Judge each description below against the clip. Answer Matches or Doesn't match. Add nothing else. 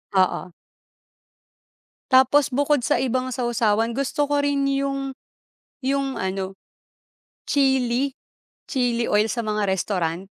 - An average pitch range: Matches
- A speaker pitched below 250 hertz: Doesn't match